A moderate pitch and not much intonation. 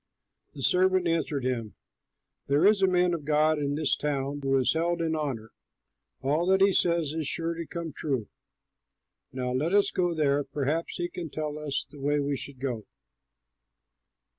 No: medium, 150 Hz; average, 3.4 semitones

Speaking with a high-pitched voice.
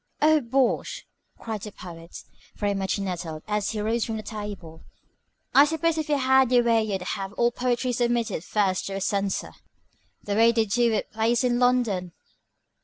Yes: high, 220 Hz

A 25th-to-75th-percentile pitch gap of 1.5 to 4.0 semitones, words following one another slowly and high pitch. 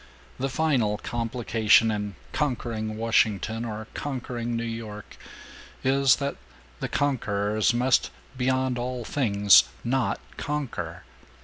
No: average, 3.2 semitones; slow, 105 wpm; low, 120 Hz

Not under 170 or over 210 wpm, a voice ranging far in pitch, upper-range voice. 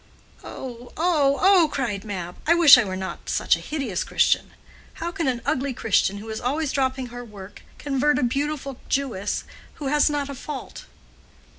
No: average, 175 wpm; average, 4.6 semitones; very high, 265 Hz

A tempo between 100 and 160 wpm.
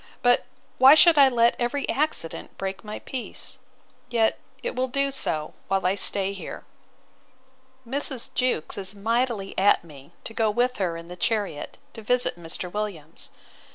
Yes: average, 155 wpm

